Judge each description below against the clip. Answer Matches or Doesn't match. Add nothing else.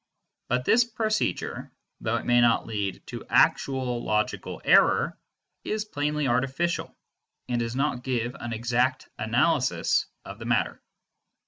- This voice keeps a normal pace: Doesn't match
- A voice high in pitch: Doesn't match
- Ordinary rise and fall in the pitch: Matches